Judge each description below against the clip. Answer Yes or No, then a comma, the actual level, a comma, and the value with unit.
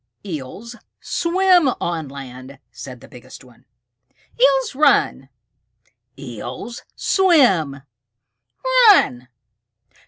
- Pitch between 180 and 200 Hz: No, medium, 155 Hz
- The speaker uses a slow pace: Yes, slow, 75 wpm